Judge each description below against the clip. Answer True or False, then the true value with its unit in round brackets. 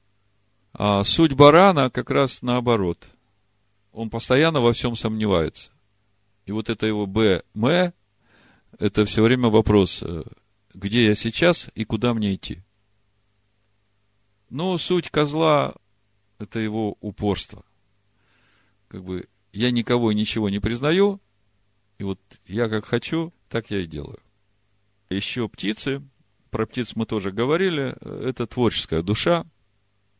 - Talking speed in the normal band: True (120 wpm)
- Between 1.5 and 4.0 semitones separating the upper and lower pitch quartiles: True (3.4 semitones)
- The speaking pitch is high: False (105 Hz)